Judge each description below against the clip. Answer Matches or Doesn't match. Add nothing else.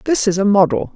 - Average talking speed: Doesn't match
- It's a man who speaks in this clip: Doesn't match